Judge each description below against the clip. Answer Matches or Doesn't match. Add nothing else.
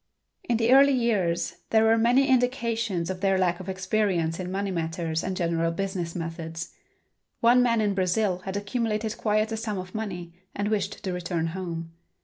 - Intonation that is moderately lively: Matches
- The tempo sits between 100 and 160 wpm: Doesn't match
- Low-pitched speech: Doesn't match